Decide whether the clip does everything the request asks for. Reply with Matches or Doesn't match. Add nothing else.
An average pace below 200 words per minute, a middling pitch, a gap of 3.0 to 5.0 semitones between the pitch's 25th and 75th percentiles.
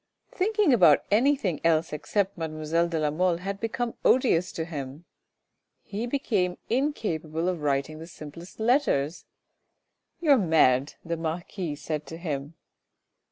Doesn't match